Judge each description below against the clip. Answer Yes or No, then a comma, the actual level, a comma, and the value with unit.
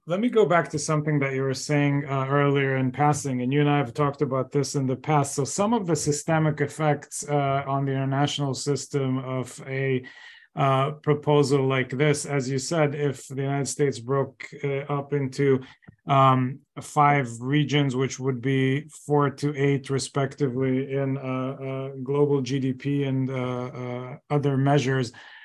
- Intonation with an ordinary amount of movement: No, narrow, 1.6 semitones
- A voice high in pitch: No, medium, 140 Hz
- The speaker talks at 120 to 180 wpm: Yes, average, 170 wpm